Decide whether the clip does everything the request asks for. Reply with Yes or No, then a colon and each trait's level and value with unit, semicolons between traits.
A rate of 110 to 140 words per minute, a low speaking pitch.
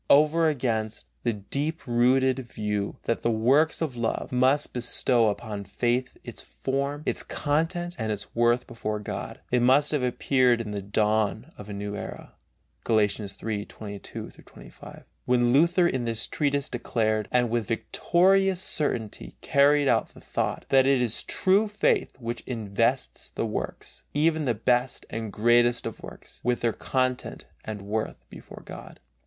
No: average, 155 wpm; low, 120 Hz